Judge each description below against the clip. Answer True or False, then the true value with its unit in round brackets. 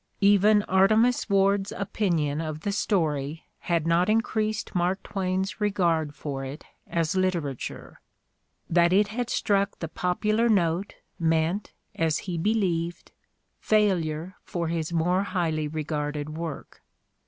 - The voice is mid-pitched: True (175 Hz)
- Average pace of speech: False (120 wpm)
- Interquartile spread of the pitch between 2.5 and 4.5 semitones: True (3.9 semitones)